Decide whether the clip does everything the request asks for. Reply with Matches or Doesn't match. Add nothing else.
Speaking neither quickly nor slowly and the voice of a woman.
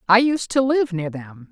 Doesn't match